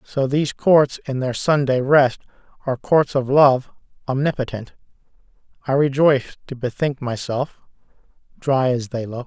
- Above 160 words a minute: No, slow, 135 wpm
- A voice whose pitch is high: No, low, 135 Hz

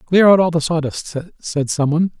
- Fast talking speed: Yes, fast, 220 wpm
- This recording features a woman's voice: No, male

